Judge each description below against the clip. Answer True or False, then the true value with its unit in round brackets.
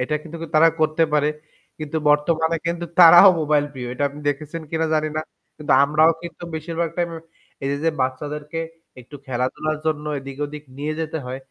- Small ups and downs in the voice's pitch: True (2.1 semitones)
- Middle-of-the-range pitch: True (155 Hz)